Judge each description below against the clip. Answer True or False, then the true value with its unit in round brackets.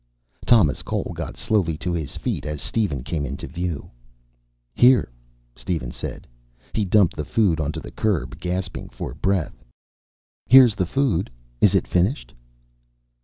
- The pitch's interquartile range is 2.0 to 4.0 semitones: False (5.5 semitones)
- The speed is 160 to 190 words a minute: False (140 wpm)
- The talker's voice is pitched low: True (90 Hz)